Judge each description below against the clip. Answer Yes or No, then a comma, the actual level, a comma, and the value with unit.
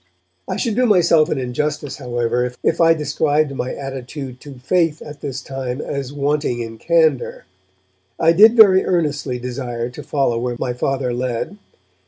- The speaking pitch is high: No, medium, 140 Hz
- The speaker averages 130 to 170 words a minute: Yes, average, 160 wpm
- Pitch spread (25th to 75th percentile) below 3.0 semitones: No, average, 4.1 semitones